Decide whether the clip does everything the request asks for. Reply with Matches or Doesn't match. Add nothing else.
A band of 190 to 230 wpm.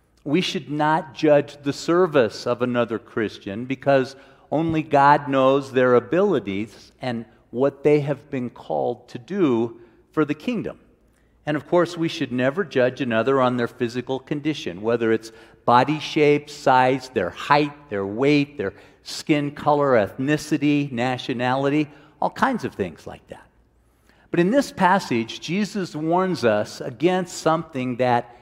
Doesn't match